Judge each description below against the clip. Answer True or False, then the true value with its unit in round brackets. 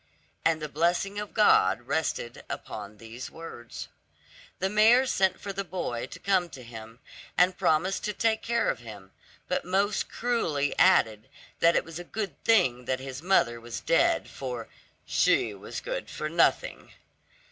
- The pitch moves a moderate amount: False (8.5 semitones)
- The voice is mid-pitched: True (160 Hz)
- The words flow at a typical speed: True (160 wpm)